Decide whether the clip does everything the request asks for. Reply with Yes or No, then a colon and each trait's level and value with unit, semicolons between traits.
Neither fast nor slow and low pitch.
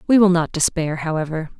No: average, 190 wpm; medium, 170 Hz